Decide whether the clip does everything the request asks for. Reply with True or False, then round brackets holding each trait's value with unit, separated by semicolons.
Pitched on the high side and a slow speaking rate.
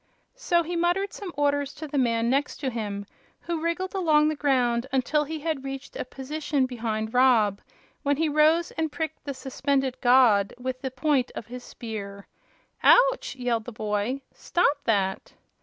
False (270 Hz; 165 wpm)